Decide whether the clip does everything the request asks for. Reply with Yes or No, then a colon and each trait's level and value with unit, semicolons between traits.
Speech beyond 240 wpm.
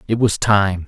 No: fast, 205 wpm